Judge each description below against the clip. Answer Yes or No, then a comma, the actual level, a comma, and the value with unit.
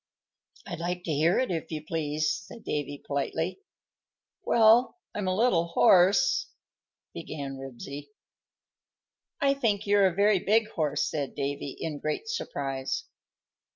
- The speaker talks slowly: Yes, slow, 130 wpm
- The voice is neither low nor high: Yes, medium, 165 Hz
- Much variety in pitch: Yes, wide, 6.0 semitones